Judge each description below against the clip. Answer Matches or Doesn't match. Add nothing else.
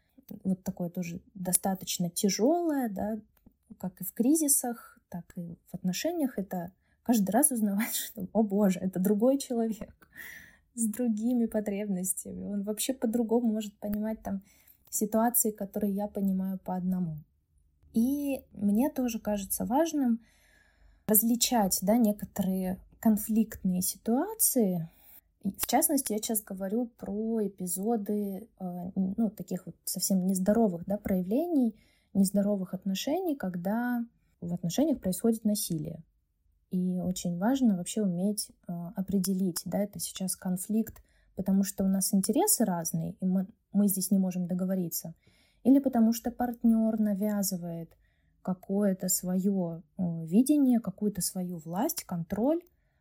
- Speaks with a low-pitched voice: Doesn't match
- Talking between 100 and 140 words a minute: Matches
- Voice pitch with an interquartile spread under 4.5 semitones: Matches